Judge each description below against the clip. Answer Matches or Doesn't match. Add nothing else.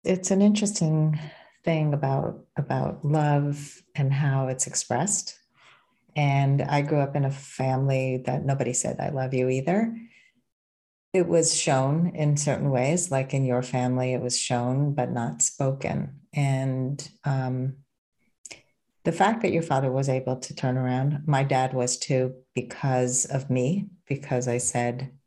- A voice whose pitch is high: Doesn't match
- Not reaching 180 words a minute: Matches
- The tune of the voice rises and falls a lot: Doesn't match